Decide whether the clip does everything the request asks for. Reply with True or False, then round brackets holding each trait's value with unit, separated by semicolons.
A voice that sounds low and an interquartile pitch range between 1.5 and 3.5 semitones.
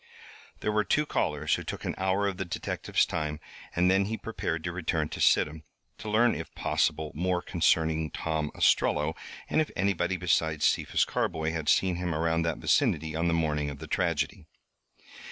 True (85 Hz; 3.1 semitones)